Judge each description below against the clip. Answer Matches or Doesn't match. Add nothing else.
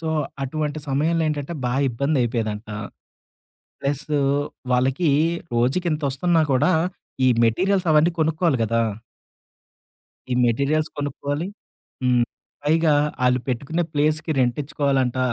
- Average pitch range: Matches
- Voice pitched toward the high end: Doesn't match